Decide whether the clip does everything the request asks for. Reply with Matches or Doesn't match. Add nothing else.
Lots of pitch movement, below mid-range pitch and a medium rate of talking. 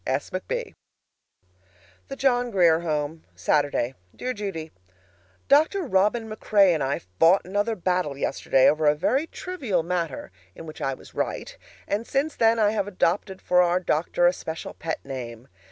Doesn't match